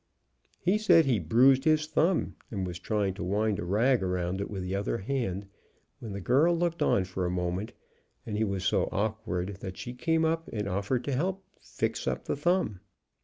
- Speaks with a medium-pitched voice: No, low, 110 Hz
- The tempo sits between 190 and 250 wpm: Yes, average, 200 wpm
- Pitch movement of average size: No, wide, 7.3 semitones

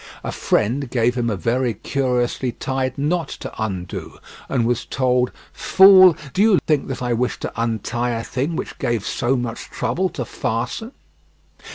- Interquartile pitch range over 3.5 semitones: No, average, 2.9 semitones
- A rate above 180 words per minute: No, average, 165 wpm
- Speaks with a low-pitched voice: Yes, low, 125 Hz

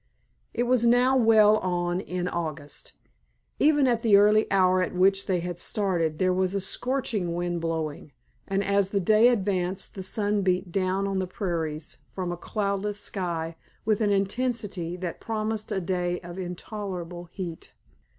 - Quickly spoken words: No, average, 160 wpm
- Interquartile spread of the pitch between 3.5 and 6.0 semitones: No, average, 3.1 semitones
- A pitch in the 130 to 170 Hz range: No, high, 190 Hz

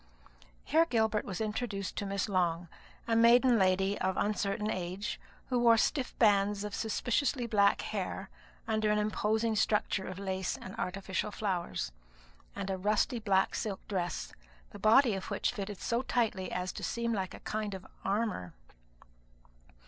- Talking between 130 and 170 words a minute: Yes, average, 155 wpm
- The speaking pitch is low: No, high, 210 Hz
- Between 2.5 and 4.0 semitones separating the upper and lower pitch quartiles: Yes, average, 2.9 semitones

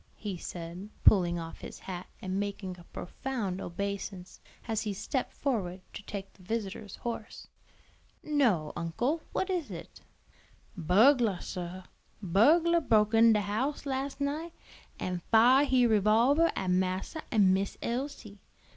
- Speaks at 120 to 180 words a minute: Yes, average, 140 wpm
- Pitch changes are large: Yes, wide, 5.8 semitones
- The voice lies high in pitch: Yes, high, 210 Hz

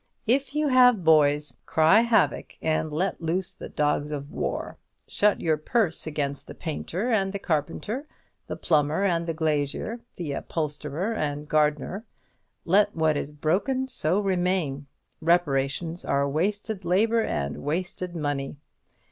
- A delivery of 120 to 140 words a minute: Yes, slow, 135 wpm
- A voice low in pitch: No, medium, 165 Hz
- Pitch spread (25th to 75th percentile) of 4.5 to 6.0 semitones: Yes, average, 5.1 semitones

